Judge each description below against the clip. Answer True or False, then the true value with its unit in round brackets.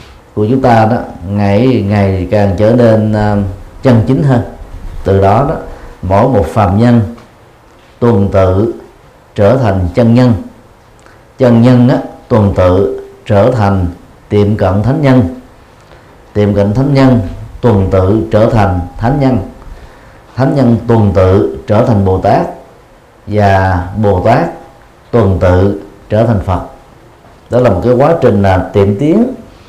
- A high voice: False (105 Hz)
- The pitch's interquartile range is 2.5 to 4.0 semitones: True (3.6 semitones)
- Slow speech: True (145 wpm)